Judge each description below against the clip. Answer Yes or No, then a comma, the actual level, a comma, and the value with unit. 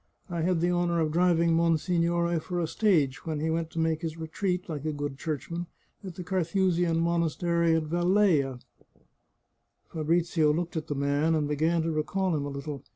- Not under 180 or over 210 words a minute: Yes, average, 185 wpm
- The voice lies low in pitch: No, medium, 165 Hz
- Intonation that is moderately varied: No, narrow, 2.0 semitones